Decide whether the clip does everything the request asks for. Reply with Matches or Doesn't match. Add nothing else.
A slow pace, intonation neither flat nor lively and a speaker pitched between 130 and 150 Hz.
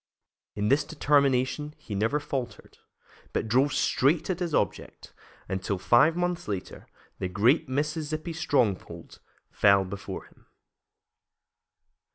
Doesn't match